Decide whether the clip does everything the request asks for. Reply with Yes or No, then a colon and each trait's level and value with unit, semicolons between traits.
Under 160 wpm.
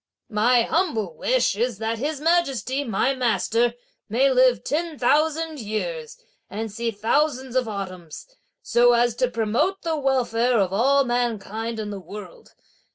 Yes: average, 145 wpm